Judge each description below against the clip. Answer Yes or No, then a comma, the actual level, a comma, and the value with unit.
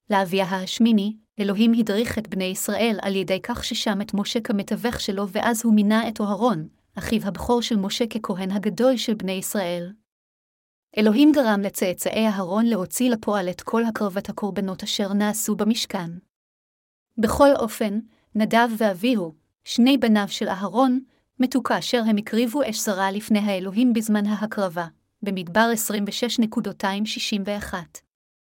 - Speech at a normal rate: Yes, average, 130 wpm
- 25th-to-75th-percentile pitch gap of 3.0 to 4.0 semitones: No, narrow, 2.5 semitones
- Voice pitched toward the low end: No, high, 215 Hz